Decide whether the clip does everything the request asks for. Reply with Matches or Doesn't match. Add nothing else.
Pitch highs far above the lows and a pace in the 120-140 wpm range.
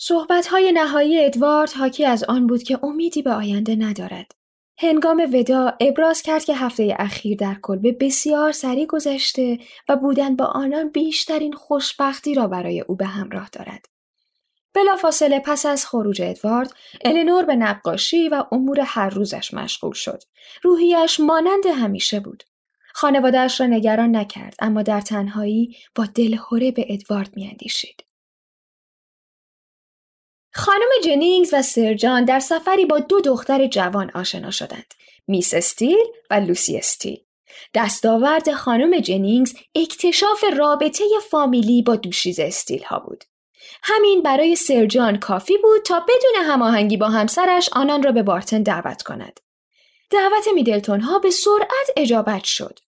Matches